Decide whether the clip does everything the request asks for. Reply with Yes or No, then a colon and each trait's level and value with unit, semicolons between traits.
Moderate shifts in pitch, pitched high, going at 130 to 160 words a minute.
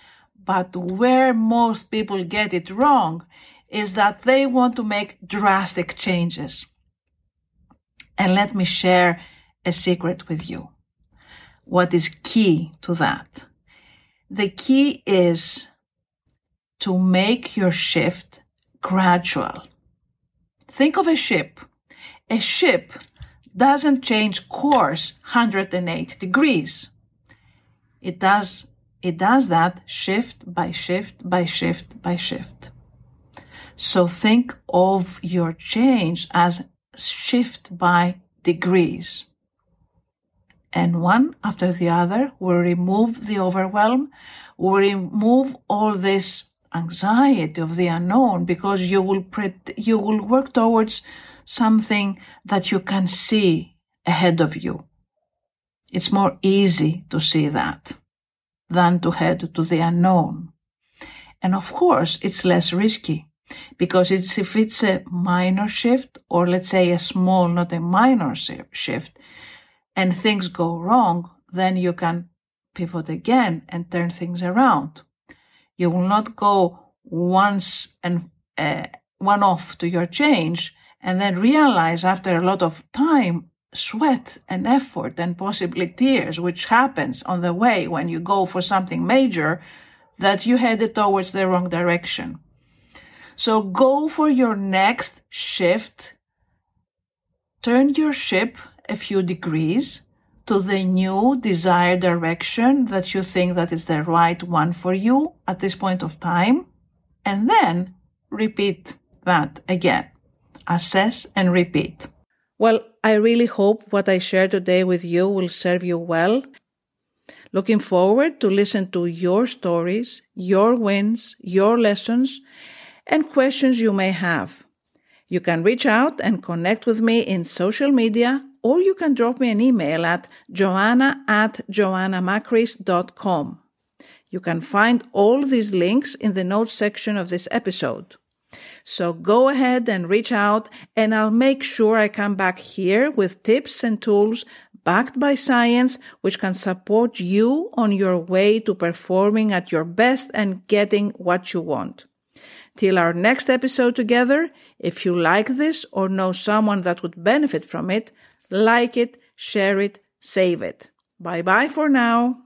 Yes: average, 4.7 semitones; high, 195 Hz; average, 135 wpm